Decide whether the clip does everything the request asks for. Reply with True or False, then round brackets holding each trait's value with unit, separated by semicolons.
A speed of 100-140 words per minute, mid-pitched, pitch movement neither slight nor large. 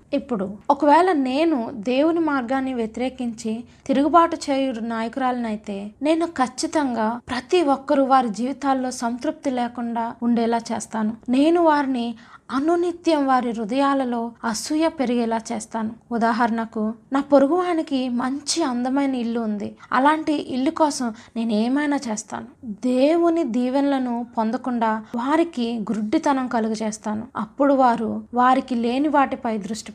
False (110 wpm; 255 Hz; 3.6 semitones)